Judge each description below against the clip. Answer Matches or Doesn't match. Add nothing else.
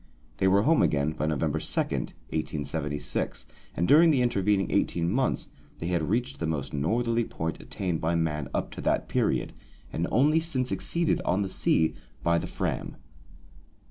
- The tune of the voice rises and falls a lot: Matches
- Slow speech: Doesn't match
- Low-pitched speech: Matches